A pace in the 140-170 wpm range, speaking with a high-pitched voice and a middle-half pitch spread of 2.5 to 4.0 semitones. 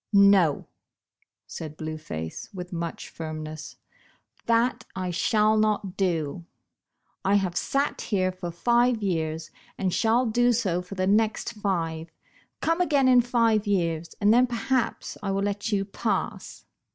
No: average, 145 wpm; high, 195 Hz; average, 5.1 semitones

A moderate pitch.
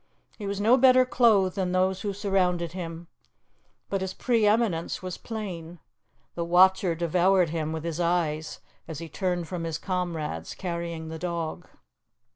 Yes: medium, 180 Hz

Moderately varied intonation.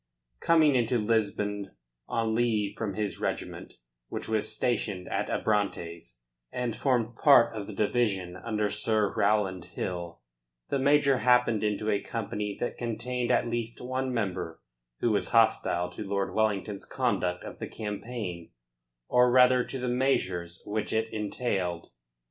Yes: average, 3.5 semitones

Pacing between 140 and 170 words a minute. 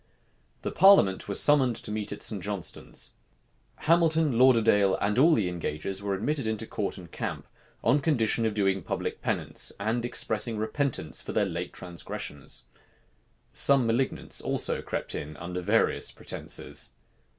Yes: average, 145 wpm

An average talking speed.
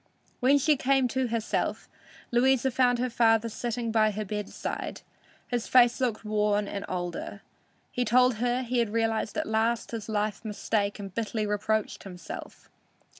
Yes: average, 150 wpm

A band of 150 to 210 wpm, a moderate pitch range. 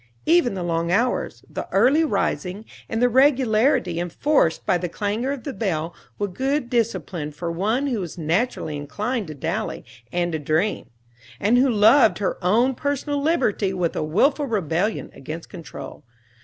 No: average, 160 wpm; wide, 6.7 semitones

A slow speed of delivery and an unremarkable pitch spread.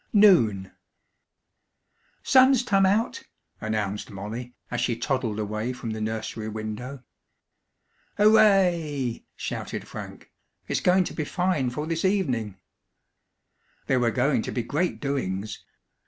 No: slow, 120 wpm; wide, 8.6 semitones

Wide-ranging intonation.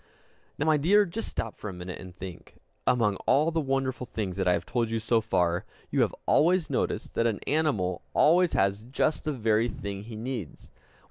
Yes: wide, 7.0 semitones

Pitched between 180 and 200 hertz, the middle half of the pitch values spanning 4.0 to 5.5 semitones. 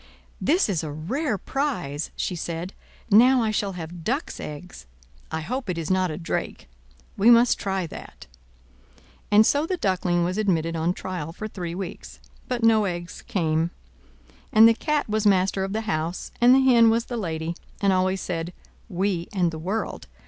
Yes: high, 190 Hz; average, 4.9 semitones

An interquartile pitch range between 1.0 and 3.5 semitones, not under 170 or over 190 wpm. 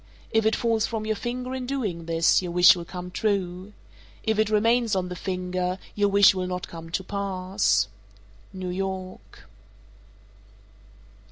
No: average, 3.2 semitones; average, 155 wpm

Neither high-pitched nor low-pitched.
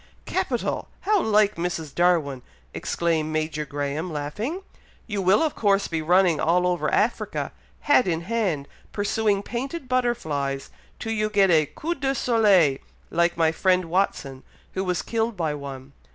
Yes: medium, 180 Hz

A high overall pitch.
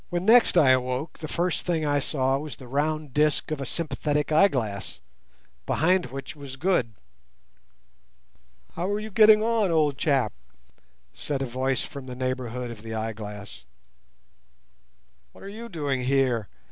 No: medium, 140 Hz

